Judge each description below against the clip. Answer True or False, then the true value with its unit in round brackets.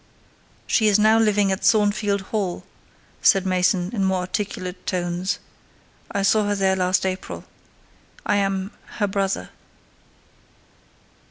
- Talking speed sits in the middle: False (120 wpm)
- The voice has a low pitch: False (195 Hz)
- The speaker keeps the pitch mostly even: True (1.8 semitones)